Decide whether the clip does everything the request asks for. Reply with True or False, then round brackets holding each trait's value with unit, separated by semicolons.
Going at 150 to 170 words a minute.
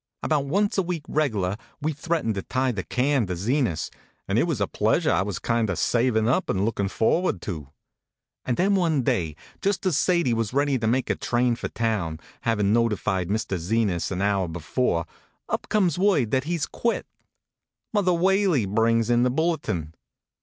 False (195 wpm)